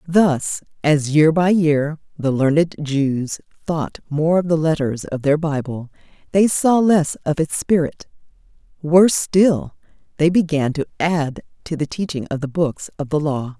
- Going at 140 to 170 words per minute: Yes, average, 165 wpm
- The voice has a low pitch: No, medium, 155 Hz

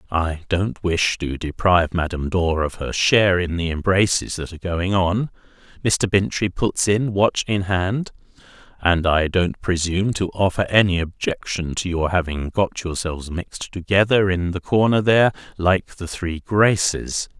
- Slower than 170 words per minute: Yes, average, 160 wpm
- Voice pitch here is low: Yes, very low, 90 Hz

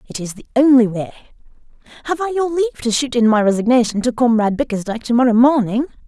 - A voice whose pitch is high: Yes, high, 245 Hz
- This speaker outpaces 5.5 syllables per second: Yes, 6.5 syllables/s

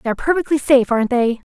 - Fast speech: Yes, fast, 235 wpm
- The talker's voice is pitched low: No, very high, 260 Hz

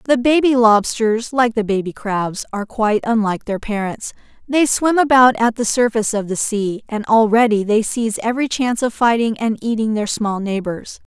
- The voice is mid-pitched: No, high, 225 Hz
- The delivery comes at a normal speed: Yes, average, 185 wpm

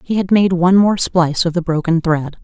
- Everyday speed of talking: No, fast, 245 wpm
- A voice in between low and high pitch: Yes, medium, 175 Hz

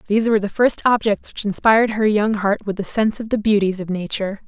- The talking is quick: Yes, fast, 240 wpm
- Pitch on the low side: No, high, 210 Hz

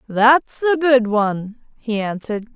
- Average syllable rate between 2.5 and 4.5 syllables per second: Yes, 4.3 syllables/s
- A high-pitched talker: Yes, high, 235 Hz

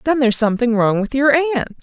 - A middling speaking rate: No, fast, 230 wpm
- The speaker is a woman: Yes, female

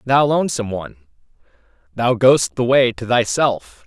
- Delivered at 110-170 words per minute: Yes, average, 140 wpm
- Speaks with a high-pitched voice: No, low, 120 Hz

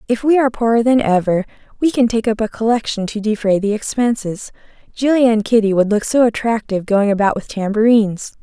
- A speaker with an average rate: Yes, average, 190 wpm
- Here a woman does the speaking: Yes, female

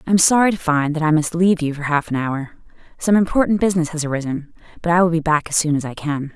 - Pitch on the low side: No, medium, 160 Hz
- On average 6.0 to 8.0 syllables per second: Yes, 6.7 syllables/s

